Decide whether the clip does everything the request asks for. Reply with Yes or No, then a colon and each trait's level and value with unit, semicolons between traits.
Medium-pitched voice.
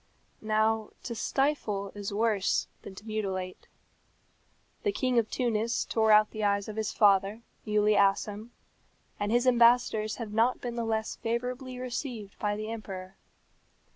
No: high, 220 Hz